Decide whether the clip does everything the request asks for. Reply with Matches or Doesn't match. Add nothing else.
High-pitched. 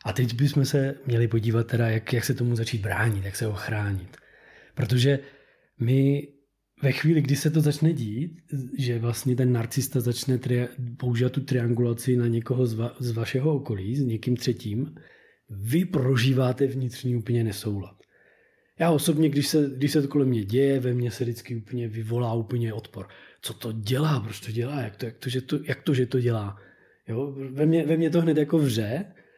Doesn't match